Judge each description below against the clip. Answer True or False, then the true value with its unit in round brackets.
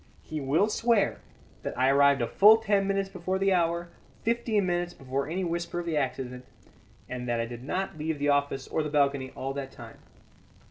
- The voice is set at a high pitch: False (155 Hz)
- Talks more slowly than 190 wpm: False (195 wpm)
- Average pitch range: False (5.9 semitones)